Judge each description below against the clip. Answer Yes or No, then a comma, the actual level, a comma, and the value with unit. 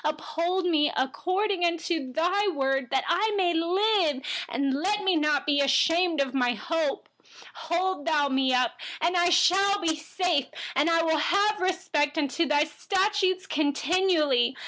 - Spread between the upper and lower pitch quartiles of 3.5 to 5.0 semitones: Yes, average, 4.4 semitones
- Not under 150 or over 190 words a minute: No, average, 140 wpm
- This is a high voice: Yes, very high, 330 Hz